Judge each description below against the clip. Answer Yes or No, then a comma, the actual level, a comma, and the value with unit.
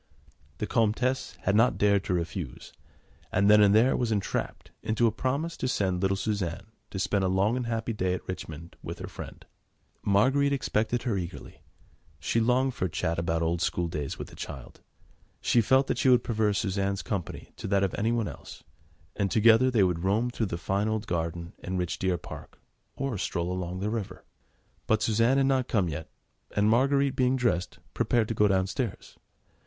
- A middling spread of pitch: Yes, average, 4.3 semitones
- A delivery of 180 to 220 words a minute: Yes, average, 190 wpm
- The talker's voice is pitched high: No, low, 105 Hz